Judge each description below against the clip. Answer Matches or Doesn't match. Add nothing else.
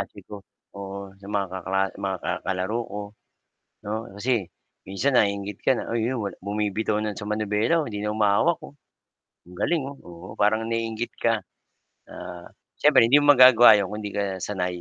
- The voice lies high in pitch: Doesn't match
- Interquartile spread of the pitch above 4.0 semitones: Doesn't match